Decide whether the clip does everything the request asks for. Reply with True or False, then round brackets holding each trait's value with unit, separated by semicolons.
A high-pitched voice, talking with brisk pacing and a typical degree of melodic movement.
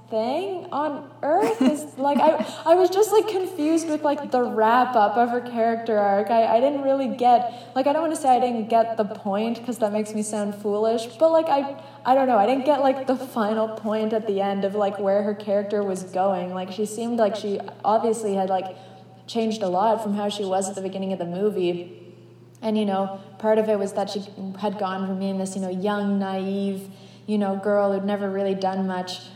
True (215 Hz; 230 wpm; 4.2 semitones)